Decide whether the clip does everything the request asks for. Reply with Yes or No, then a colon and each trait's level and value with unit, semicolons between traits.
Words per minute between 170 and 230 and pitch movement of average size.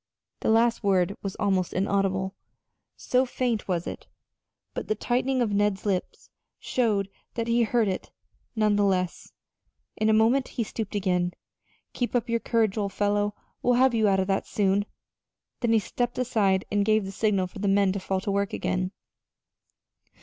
Yes: average, 180 wpm; average, 3.0 semitones